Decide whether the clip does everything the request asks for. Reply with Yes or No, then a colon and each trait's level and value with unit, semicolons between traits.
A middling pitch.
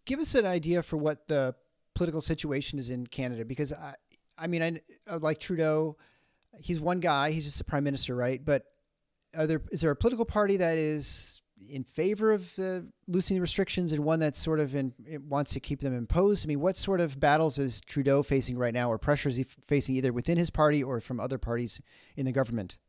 Yes: medium, 150 Hz